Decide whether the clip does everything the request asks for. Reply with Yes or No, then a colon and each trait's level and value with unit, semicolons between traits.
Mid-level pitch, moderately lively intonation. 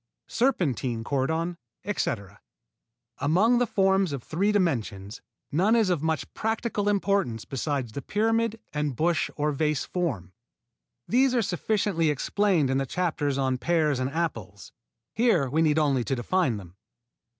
No: medium, 160 Hz; wide, 7.0 semitones